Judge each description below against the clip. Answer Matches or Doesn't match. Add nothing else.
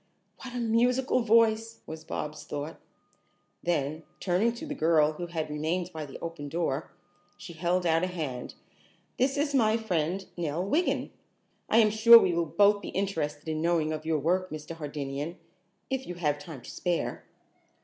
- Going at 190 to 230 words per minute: Doesn't match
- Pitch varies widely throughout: Matches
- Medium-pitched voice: Matches